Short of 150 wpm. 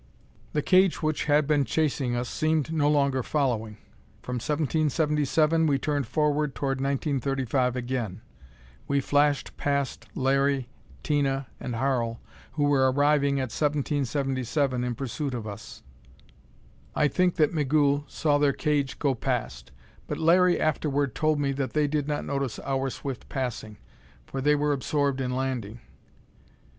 Yes: average, 140 wpm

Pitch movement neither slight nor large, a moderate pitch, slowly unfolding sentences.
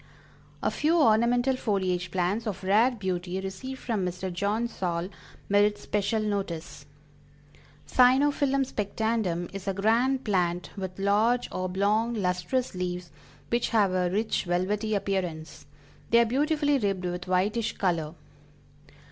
No: average, 4.3 semitones; high, 200 Hz; slow, 125 wpm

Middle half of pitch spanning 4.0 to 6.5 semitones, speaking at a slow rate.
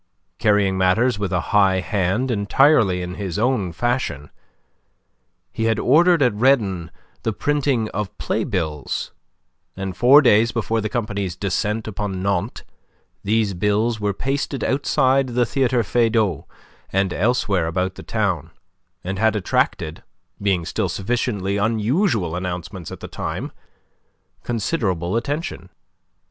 Yes: average, 4.4 semitones; slow, 125 wpm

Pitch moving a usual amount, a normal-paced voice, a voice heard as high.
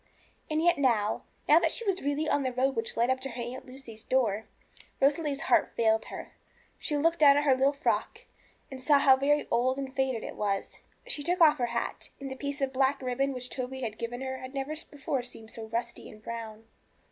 No: average, 3.1 semitones; fast, 220 wpm; very high, 265 Hz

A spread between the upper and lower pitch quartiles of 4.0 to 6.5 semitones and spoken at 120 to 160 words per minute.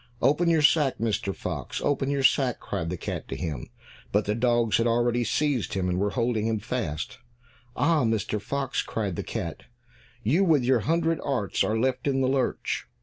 No: average, 4.7 semitones; average, 190 wpm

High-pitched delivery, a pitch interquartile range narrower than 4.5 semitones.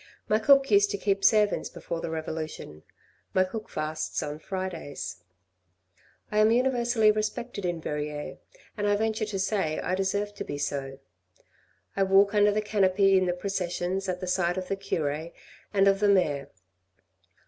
Yes: high, 195 Hz; average, 3.9 semitones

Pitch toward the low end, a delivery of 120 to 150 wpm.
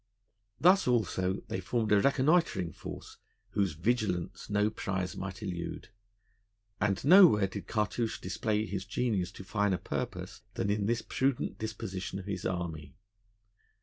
Yes: low, 100 Hz; slow, 135 wpm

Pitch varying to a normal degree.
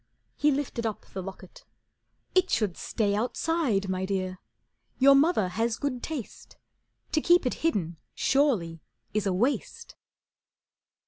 No: wide, 7.0 semitones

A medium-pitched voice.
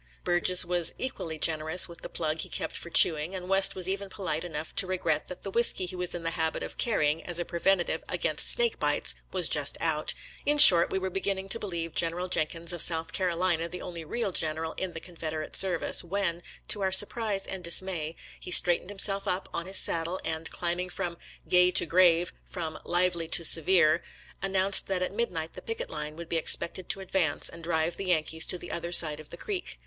Yes: medium, 175 Hz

